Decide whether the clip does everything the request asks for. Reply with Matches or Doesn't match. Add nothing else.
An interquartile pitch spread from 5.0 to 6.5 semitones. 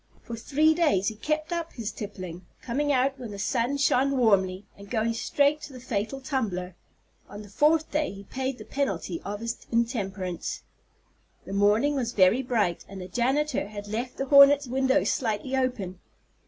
Matches